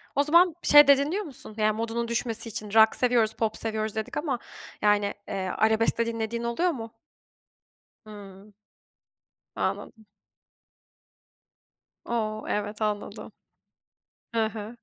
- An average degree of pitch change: No, narrow, 1.8 semitones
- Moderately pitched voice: No, high, 225 Hz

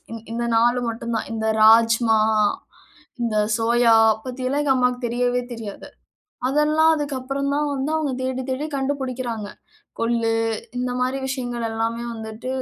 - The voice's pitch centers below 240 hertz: No, high, 245 Hz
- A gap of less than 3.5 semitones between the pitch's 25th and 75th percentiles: Yes, narrow, 2.6 semitones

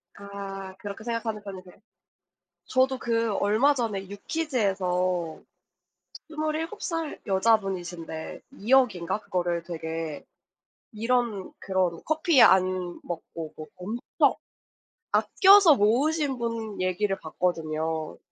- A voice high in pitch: Yes, high, 200 Hz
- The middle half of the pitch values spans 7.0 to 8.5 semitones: No, average, 5.1 semitones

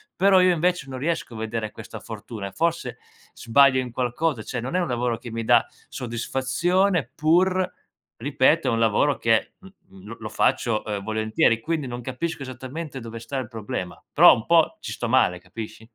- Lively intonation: Yes, wide, 6.1 semitones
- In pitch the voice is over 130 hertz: No, low, 125 Hz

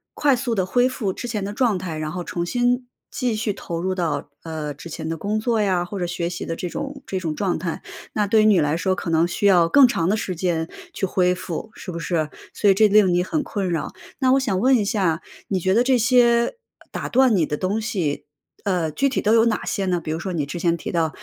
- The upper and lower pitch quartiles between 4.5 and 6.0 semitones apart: Yes, average, 5.0 semitones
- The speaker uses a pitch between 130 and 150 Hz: No, high, 190 Hz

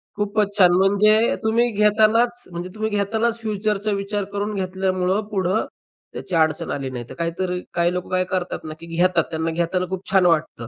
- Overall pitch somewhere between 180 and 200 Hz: Yes, high, 190 Hz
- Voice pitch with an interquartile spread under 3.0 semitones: No, average, 3.3 semitones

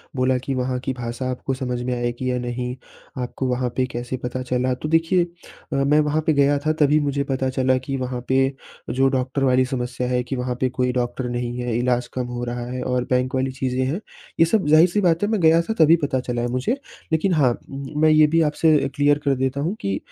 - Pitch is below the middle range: Yes, low, 130 Hz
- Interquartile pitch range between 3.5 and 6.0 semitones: No, average, 2.9 semitones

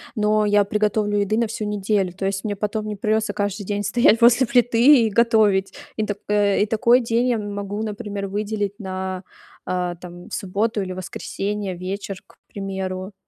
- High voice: Yes, high, 205 Hz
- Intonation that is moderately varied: No, narrow, 1.9 semitones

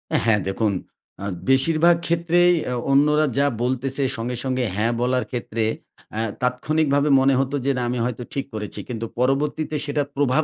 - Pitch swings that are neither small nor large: Yes, average, 3.3 semitones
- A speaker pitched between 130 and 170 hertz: Yes, low, 135 Hz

